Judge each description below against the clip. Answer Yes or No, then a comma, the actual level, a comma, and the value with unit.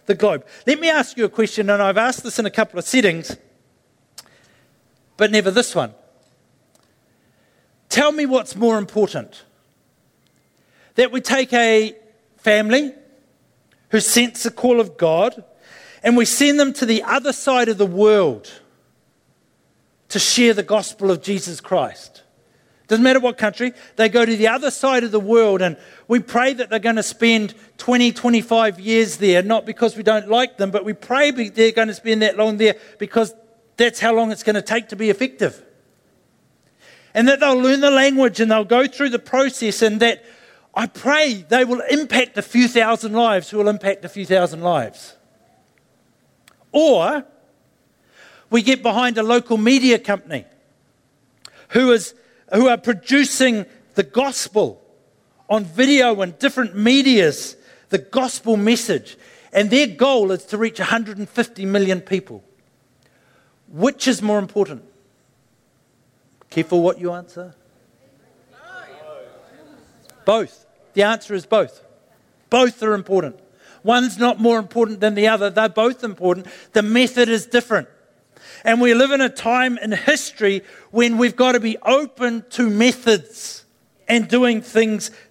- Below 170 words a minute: Yes, average, 155 wpm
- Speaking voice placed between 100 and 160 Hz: No, high, 225 Hz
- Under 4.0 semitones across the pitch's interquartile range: Yes, average, 3.4 semitones